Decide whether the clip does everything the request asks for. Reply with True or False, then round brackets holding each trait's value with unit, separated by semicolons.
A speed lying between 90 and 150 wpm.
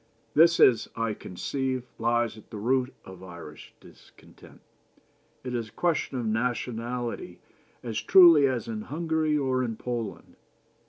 True (140 wpm)